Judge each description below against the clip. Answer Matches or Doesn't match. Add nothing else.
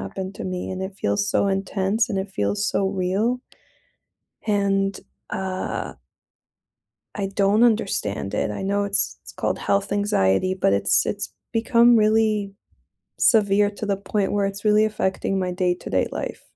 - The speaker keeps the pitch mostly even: Matches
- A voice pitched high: Matches